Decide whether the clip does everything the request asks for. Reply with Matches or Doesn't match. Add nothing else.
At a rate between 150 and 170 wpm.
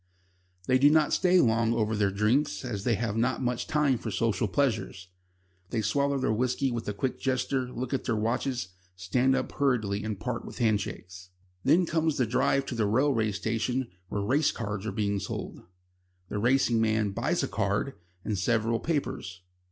Doesn't match